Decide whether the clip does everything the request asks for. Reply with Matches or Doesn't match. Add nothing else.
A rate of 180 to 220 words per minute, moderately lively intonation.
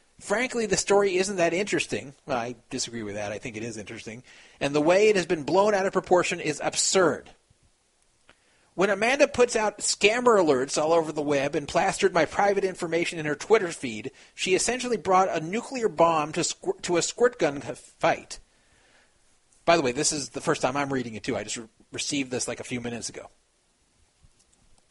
Doesn't match